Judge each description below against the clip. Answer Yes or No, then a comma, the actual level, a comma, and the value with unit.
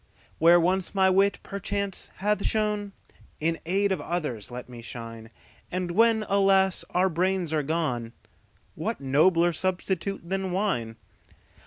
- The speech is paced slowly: Yes, slow, 120 wpm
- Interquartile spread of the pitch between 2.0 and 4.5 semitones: No, average, 5.0 semitones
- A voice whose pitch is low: No, medium, 180 Hz